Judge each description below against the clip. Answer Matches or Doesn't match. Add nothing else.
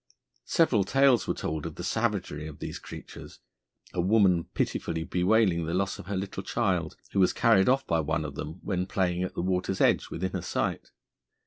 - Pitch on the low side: Matches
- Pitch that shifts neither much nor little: Matches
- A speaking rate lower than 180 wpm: Doesn't match